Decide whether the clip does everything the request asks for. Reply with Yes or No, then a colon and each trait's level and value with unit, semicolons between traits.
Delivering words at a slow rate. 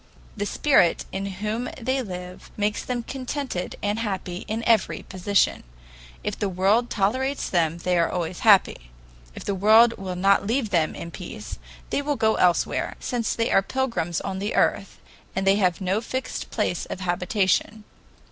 No: average, 165 wpm